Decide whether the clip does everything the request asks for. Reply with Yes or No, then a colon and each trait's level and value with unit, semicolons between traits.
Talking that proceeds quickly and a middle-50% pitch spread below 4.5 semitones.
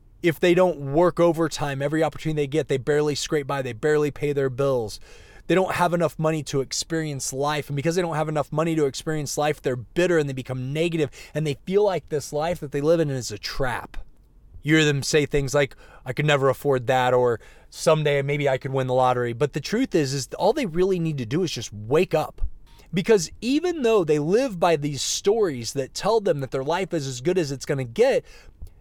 Yes: fast, 230 wpm; average, 3.7 semitones